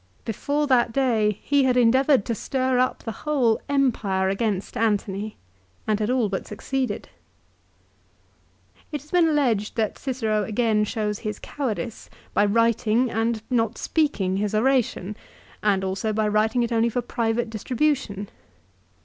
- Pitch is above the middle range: Yes, high, 225 Hz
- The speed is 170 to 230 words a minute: No, average, 140 wpm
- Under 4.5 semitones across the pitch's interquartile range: Yes, average, 3.4 semitones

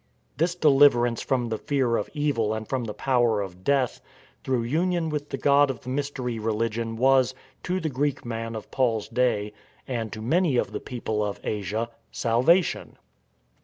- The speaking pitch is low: Yes, low, 125 Hz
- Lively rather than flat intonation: No, average, 3.9 semitones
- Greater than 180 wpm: No, average, 175 wpm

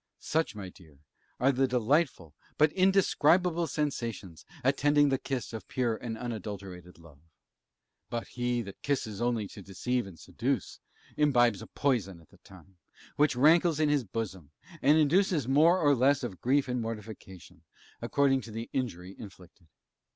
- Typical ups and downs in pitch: No, wide, 6.5 semitones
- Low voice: Yes, low, 120 Hz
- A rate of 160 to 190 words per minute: No, average, 150 wpm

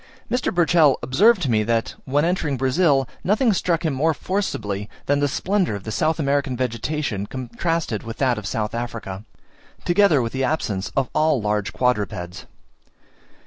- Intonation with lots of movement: Yes, wide, 6.4 semitones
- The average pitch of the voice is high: No, low, 135 Hz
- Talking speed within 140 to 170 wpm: Yes, average, 160 wpm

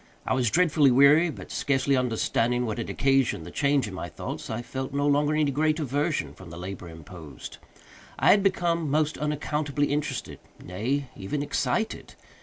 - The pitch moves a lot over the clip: No, average, 4.7 semitones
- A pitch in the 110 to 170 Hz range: Yes, medium, 140 Hz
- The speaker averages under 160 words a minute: No, average, 165 wpm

